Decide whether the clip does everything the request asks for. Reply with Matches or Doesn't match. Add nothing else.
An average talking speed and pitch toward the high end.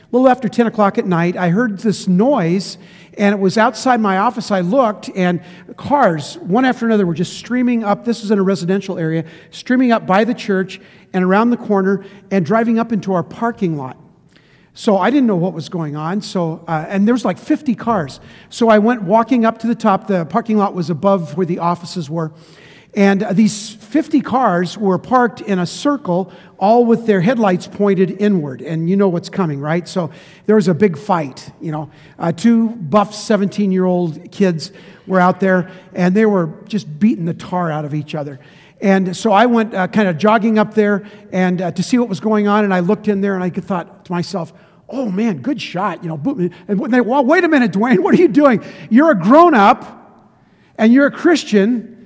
Doesn't match